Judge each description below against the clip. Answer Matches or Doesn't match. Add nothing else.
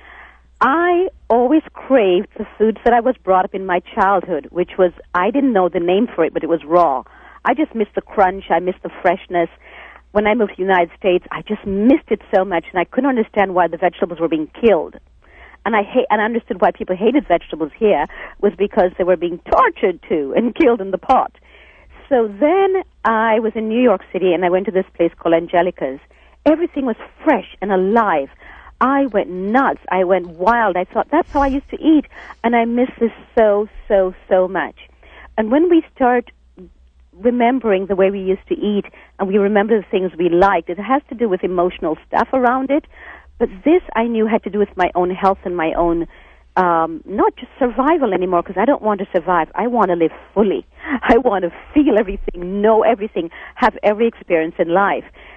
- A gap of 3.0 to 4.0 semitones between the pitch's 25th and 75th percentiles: Doesn't match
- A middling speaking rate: Doesn't match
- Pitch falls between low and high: Doesn't match